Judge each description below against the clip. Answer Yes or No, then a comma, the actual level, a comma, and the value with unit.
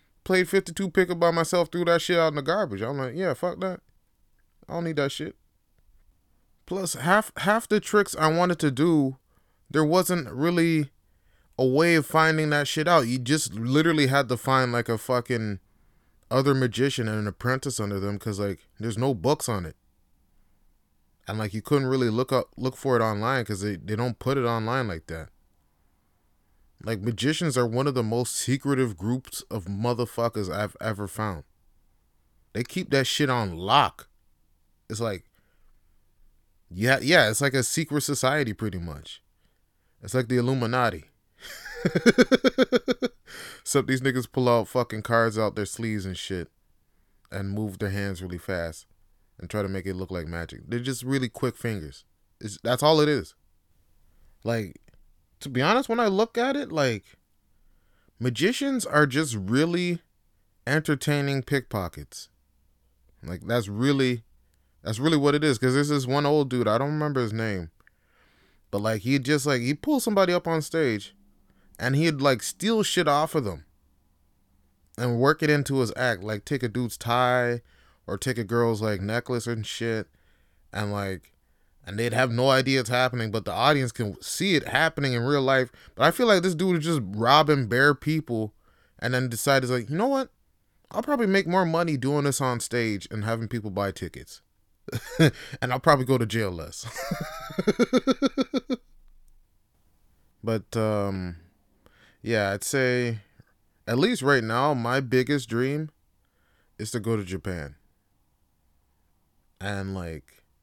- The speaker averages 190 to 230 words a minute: No, average, 165 wpm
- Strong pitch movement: Yes, wide, 7.1 semitones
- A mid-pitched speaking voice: No, low, 120 Hz